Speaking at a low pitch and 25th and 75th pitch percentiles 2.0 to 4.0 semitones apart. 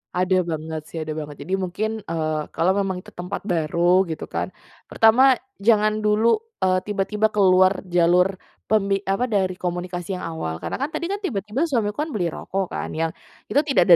No: high, 190 Hz; average, 3.5 semitones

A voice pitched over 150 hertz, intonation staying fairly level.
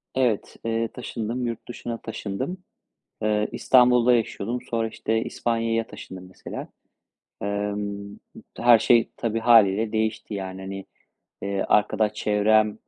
No: low, 110 Hz; narrow, 2.3 semitones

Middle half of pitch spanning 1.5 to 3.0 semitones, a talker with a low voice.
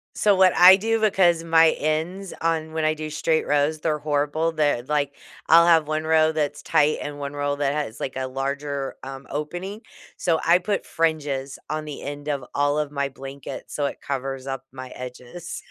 No: narrow, 2.6 semitones; medium, 150 Hz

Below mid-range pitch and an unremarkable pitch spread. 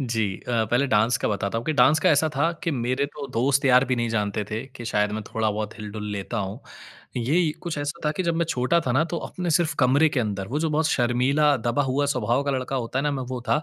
Yes: low, 130 Hz; average, 4.3 semitones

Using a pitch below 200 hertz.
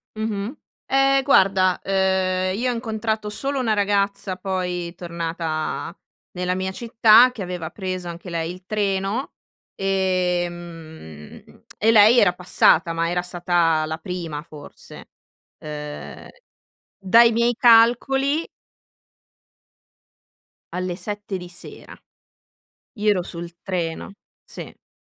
Yes: medium, 185 Hz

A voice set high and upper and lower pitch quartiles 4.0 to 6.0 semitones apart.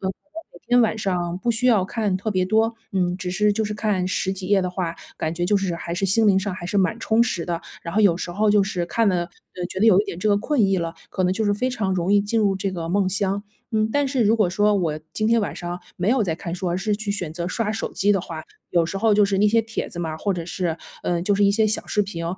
No: high, 195 Hz; average, 3.1 semitones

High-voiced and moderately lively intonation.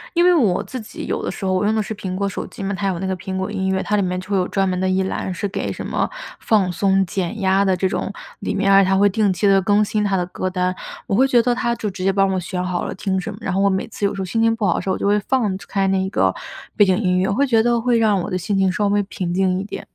No: high, 195 Hz; narrow, 1.9 semitones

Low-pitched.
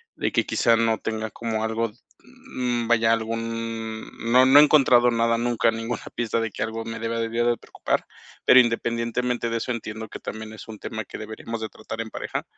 Yes: low, 115 Hz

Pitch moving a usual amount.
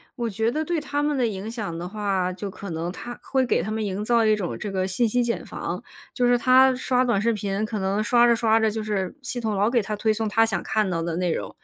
Yes: average, 3.5 semitones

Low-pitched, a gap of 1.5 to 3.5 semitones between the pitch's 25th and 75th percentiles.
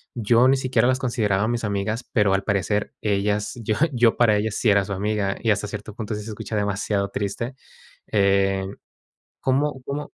Yes: low, 105 Hz; average, 2.8 semitones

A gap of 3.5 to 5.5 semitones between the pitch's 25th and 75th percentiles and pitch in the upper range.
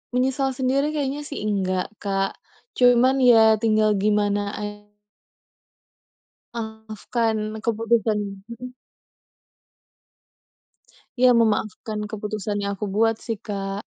No: average, 2.8 semitones; high, 220 Hz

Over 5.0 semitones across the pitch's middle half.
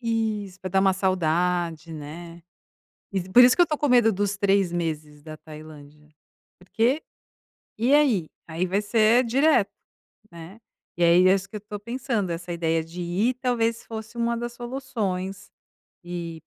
Yes: wide, 5.4 semitones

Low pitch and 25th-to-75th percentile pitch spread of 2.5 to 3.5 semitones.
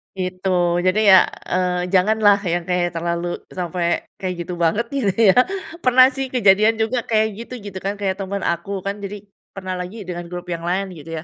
No: medium, 185 Hz; average, 2.9 semitones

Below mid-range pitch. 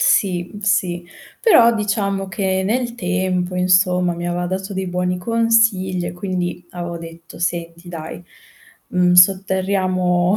No: medium, 185 Hz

